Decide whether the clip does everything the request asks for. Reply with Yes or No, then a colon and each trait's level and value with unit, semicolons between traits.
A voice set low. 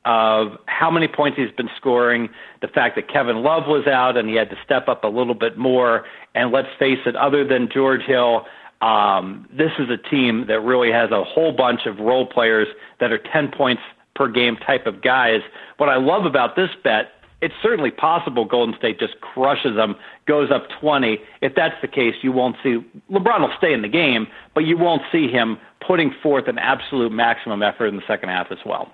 Yes: low, 125 Hz